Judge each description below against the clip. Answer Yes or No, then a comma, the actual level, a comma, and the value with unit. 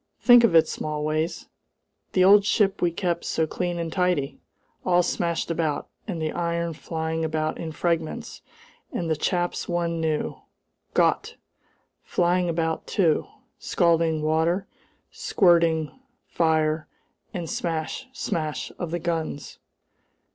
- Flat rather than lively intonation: Yes, narrow, 1.8 semitones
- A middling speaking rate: No, slow, 125 wpm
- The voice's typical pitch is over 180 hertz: No, medium, 165 Hz